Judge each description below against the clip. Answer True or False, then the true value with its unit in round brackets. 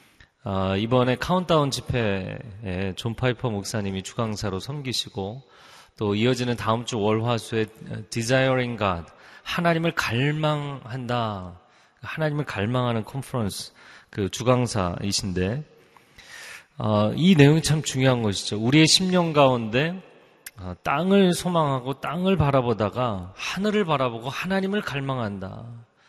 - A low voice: True (125 Hz)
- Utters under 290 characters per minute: True (275 characters per minute)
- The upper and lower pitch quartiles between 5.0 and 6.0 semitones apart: True (5.4 semitones)